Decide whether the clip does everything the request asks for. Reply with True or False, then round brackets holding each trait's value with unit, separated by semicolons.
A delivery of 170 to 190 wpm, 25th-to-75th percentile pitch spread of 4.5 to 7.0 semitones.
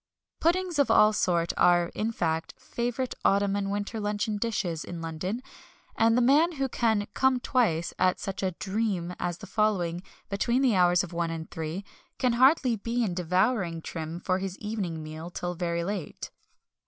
True (175 wpm; 5.0 semitones)